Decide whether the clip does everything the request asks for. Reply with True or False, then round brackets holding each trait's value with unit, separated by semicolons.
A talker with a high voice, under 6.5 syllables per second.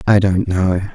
False (95 Hz; 4.3 syllables/s)